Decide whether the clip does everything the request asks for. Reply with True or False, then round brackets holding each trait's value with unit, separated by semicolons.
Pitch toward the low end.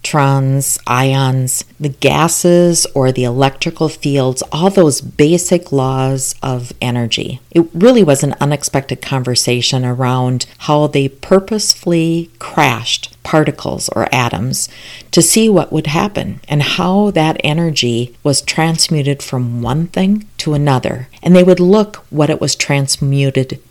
False (145 Hz)